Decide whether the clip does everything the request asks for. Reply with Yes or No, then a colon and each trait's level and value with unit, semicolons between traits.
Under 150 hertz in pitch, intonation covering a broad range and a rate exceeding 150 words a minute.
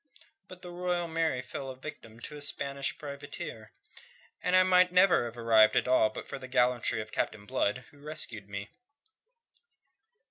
Yes: low, 135 Hz; wide, 6.4 semitones; average, 170 wpm